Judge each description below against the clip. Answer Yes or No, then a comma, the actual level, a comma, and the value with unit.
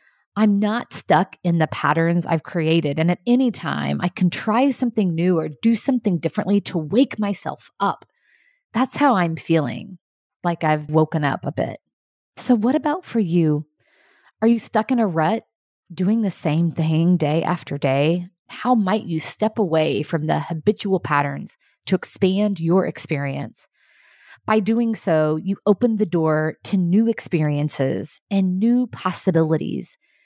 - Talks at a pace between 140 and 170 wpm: Yes, average, 155 wpm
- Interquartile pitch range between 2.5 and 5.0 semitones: No, wide, 5.4 semitones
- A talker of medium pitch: Yes, medium, 180 Hz